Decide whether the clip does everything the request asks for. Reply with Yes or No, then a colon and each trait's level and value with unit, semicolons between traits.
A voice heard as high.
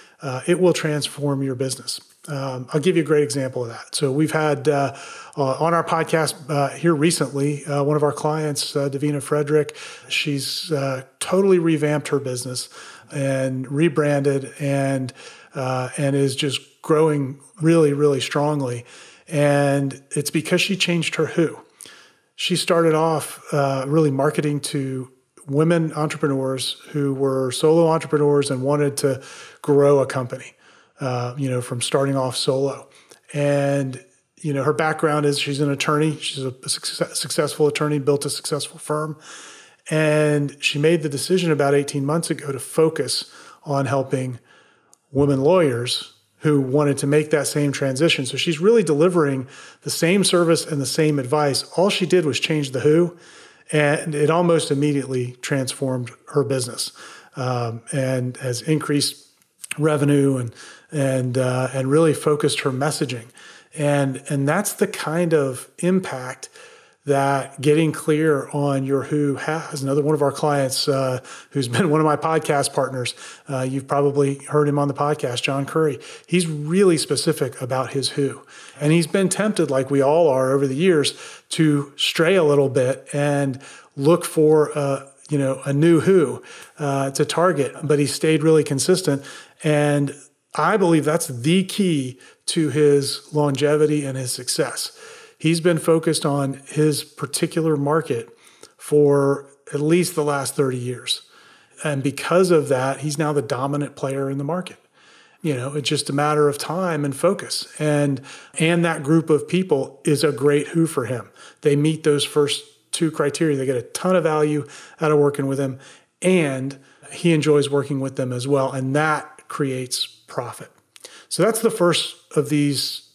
No: medium, 145 Hz